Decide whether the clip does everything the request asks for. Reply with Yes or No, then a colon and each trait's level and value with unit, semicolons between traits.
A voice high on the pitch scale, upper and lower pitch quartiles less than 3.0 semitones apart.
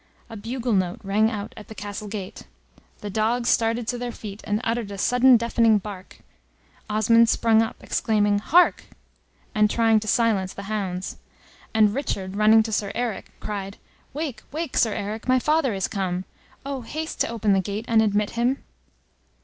Yes: high, 220 Hz; narrow, 2.5 semitones